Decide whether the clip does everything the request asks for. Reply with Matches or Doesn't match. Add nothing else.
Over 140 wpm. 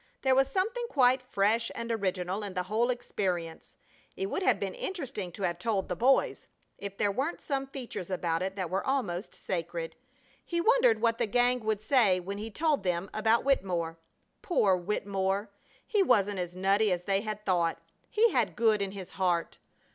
Matches